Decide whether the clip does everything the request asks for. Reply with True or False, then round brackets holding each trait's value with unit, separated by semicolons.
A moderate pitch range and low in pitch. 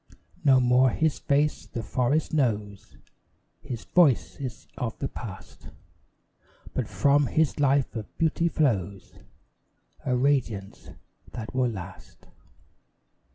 True (4.4 semitones; 130 Hz)